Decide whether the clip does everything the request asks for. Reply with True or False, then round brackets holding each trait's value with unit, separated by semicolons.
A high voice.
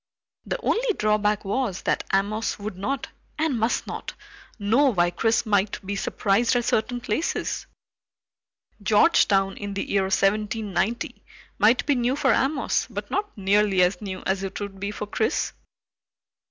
True (210 Hz)